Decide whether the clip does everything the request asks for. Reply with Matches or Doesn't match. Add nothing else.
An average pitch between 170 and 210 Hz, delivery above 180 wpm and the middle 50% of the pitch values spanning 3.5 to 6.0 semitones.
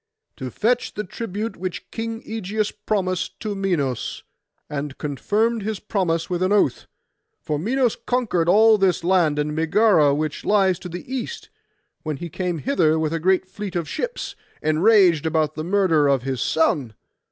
Doesn't match